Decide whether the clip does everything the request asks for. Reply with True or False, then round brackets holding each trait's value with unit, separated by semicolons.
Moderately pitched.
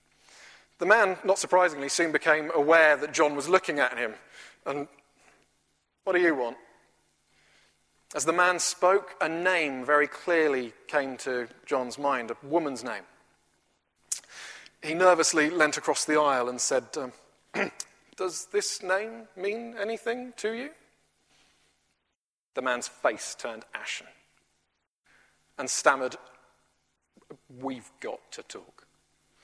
True (150 Hz)